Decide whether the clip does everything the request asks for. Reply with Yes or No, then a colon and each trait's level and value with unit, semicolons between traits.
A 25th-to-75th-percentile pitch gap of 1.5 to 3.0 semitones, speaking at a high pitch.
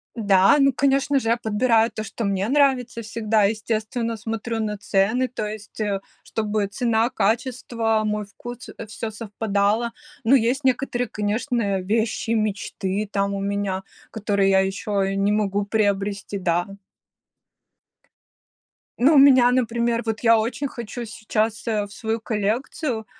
Yes: average, 2.7 semitones; high, 220 Hz